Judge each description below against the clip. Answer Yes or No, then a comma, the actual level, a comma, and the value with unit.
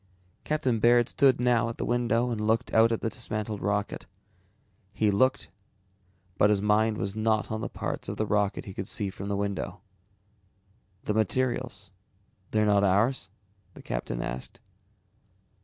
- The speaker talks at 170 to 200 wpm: No, average, 155 wpm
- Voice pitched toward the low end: Yes, low, 110 Hz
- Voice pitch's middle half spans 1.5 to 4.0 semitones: Yes, narrow, 2.6 semitones